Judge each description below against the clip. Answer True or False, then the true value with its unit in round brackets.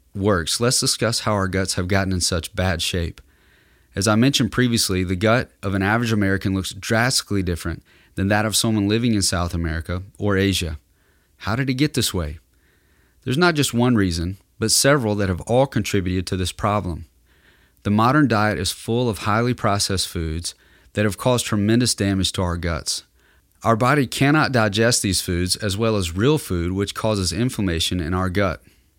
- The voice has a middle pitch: False (100 Hz)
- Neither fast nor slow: True (185 wpm)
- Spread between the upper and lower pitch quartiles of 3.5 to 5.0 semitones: True (4.2 semitones)